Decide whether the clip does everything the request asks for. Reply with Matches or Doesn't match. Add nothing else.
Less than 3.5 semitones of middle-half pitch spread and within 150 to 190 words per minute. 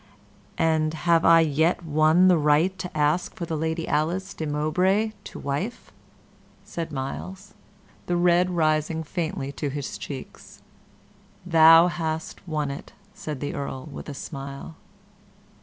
Doesn't match